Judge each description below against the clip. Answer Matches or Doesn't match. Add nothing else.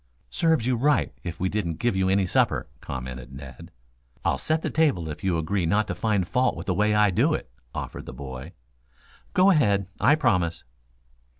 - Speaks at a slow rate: Doesn't match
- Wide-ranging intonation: Matches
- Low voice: Matches